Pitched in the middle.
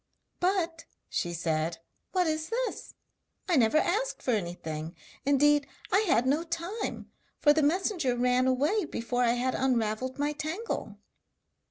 No: very high, 285 Hz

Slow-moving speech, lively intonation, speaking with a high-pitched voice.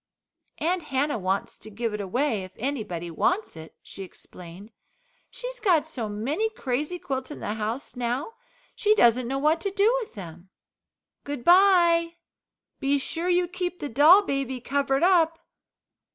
No: average, 155 wpm; wide, 7.9 semitones; very high, 280 Hz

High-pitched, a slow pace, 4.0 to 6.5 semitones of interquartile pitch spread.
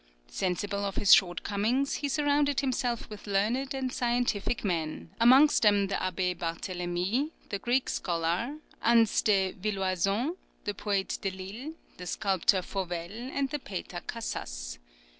Yes: high, 205 Hz; slow, 130 wpm; average, 4.9 semitones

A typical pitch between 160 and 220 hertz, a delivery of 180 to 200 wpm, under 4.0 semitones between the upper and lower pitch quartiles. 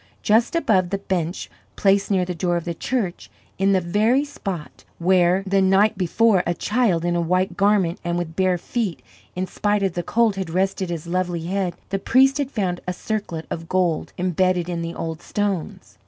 Yes: medium, 185 Hz; average, 195 wpm; narrow, 2.6 semitones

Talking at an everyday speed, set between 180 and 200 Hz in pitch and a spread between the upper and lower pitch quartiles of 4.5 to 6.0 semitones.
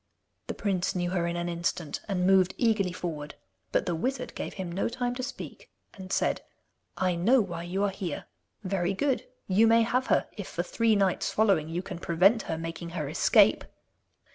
No: average, 190 wpm; medium, 185 Hz; average, 3.7 semitones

